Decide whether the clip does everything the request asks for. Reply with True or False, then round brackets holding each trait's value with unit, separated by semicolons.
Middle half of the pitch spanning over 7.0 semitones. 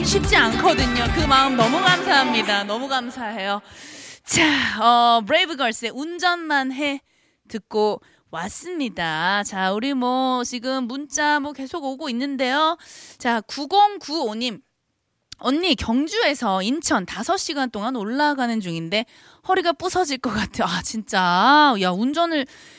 False (5.2 semitones)